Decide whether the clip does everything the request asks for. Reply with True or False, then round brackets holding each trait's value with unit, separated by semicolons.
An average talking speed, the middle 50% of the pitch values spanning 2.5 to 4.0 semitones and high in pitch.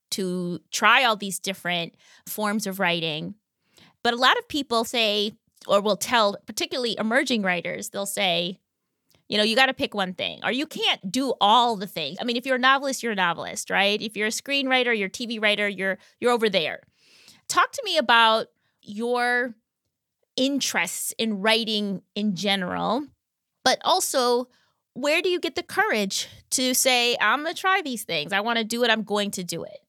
False (190 wpm; 4.4 semitones; 225 Hz)